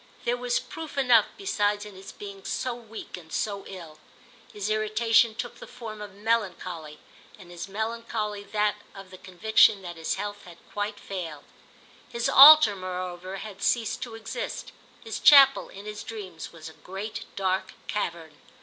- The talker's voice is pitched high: Yes, high, 205 Hz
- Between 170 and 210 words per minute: No, average, 160 wpm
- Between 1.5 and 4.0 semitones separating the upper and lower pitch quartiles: Yes, average, 3.4 semitones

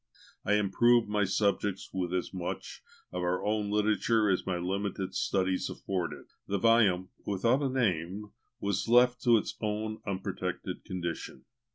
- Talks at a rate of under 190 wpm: Yes, average, 145 wpm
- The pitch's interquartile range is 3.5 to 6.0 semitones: No, average, 2.8 semitones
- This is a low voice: Yes, low, 100 Hz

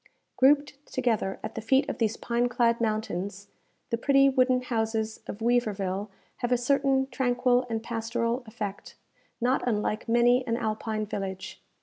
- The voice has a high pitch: Yes, high, 235 Hz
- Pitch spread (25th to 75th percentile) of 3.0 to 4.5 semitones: No, narrow, 2.6 semitones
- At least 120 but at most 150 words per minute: Yes, average, 145 wpm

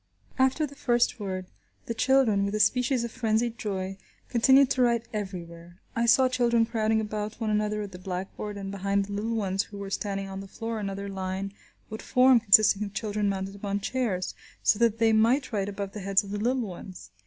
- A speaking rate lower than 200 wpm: No, fast, 205 wpm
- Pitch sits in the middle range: No, high, 210 Hz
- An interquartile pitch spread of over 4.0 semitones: No, average, 3.0 semitones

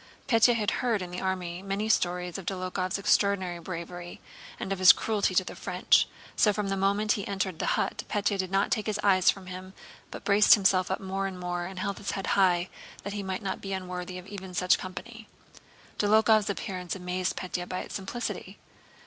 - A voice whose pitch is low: No, high, 190 Hz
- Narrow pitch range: Yes, narrow, 1.8 semitones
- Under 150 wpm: No, average, 200 wpm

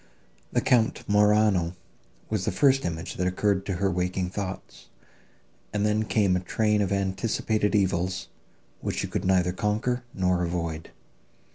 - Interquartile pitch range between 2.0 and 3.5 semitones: Yes, average, 2.7 semitones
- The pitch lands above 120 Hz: No, very low, 95 Hz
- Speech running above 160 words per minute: No, average, 145 wpm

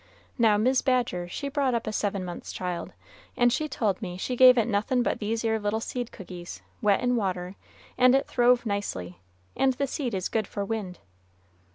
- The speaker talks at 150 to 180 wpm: No, average, 195 wpm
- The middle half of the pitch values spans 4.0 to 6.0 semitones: Yes, average, 4.3 semitones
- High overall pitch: Yes, high, 220 Hz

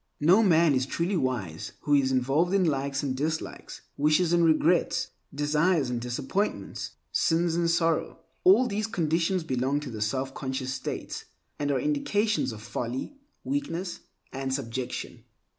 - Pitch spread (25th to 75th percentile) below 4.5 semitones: No, average, 5.0 semitones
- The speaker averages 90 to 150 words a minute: Yes, average, 140 wpm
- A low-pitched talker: No, medium, 150 Hz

